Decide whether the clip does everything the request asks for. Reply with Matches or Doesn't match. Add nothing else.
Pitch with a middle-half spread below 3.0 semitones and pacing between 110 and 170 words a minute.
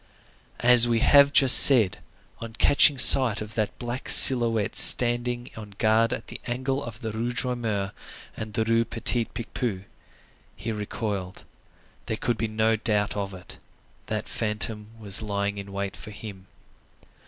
Matches